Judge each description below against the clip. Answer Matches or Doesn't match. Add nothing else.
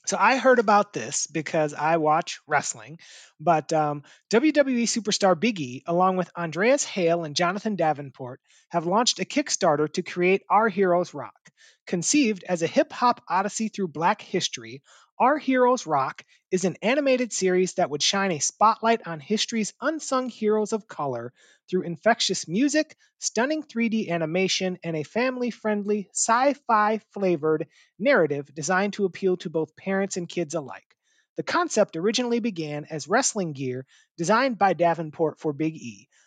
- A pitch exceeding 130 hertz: Matches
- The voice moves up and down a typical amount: Doesn't match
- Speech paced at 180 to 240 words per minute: Doesn't match